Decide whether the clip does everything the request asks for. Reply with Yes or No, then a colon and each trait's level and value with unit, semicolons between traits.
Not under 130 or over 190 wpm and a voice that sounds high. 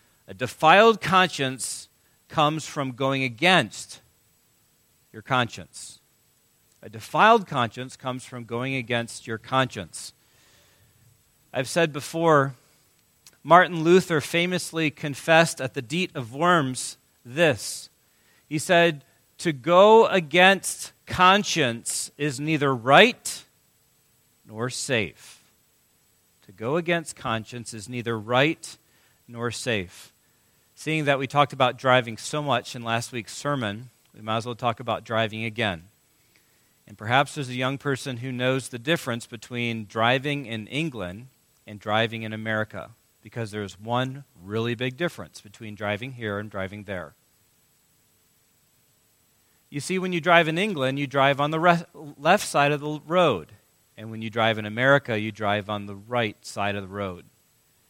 No: average, 140 wpm; low, 130 Hz